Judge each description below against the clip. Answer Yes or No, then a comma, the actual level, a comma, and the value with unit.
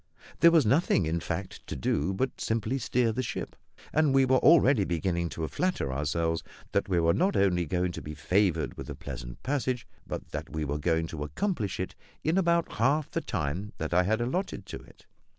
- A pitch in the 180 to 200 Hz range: No, very low, 95 Hz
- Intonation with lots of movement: Yes, wide, 8.3 semitones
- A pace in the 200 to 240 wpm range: Yes, fast, 205 wpm